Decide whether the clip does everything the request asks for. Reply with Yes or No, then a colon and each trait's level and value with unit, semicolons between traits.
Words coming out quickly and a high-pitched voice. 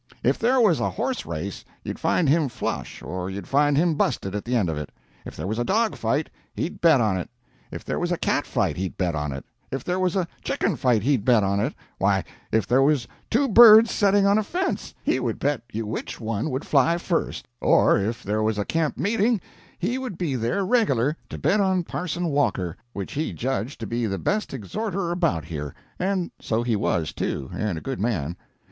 No: fast, 220 wpm; low, 135 Hz